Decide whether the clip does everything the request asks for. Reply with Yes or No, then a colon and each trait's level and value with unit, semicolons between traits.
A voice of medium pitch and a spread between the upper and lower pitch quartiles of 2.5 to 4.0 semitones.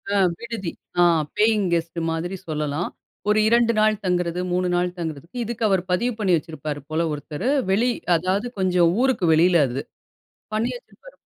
No: medium, 180 Hz; average, 4.7 semitones